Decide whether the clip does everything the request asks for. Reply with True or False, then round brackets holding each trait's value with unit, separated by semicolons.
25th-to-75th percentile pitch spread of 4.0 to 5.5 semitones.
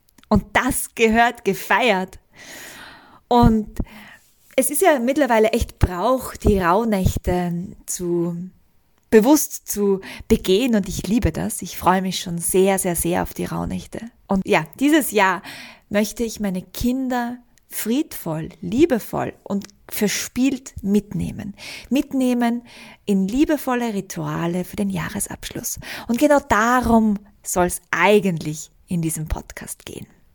True (5.0 semitones)